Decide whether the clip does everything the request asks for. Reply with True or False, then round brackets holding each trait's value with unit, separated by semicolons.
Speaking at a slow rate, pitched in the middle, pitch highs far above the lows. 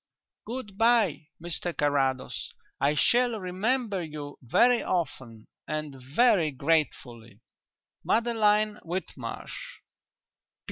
True (85 wpm; 175 Hz; 7.6 semitones)